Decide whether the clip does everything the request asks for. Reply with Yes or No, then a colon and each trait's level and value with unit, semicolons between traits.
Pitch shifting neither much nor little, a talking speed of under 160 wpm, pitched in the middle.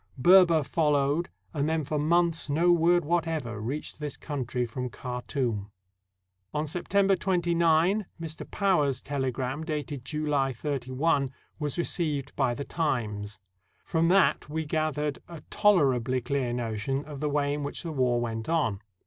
Yes: average, 4.2 semitones; average, 150 wpm; medium, 145 Hz